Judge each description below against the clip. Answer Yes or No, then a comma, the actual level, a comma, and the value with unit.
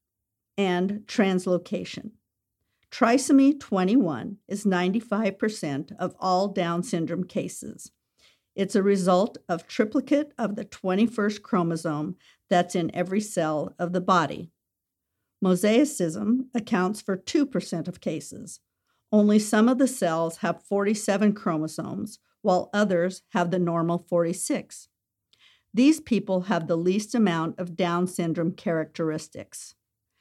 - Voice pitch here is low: No, medium, 185 Hz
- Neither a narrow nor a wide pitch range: Yes, average, 3.9 semitones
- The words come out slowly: Yes, slow, 115 wpm